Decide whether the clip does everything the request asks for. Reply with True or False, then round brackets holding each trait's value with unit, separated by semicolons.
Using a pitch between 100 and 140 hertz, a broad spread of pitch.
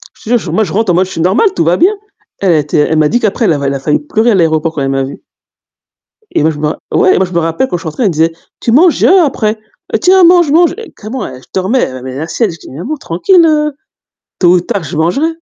False (185 Hz; 8.5 semitones)